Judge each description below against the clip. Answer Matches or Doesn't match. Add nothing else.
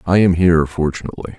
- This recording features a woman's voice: Doesn't match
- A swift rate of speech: Doesn't match